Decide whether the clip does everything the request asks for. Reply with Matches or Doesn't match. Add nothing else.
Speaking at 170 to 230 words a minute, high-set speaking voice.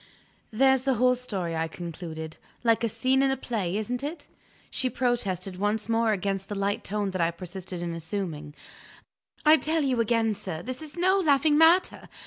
Matches